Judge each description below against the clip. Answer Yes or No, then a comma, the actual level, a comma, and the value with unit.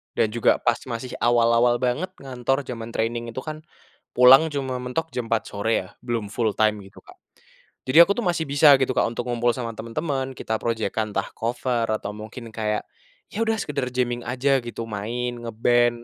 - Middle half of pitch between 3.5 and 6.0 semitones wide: No, narrow, 2.4 semitones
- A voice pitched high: No, low, 120 Hz